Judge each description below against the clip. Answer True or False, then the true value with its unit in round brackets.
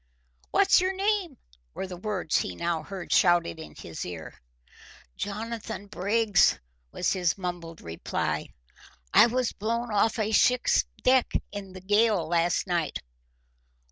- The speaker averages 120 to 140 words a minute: True (135 wpm)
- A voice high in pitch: True (200 Hz)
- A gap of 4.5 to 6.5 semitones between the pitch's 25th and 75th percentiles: True (4.8 semitones)